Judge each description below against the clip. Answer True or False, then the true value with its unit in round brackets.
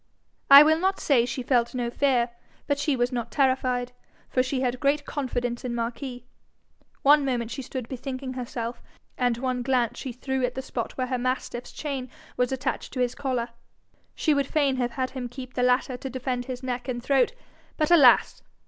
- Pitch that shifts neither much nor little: False (1.7 semitones)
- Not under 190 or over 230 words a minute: True (195 wpm)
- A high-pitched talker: True (255 Hz)